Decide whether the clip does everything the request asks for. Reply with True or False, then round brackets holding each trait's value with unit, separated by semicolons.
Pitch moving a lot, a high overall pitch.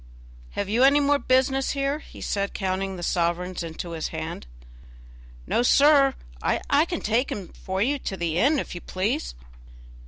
True (7.4 semitones; 210 Hz)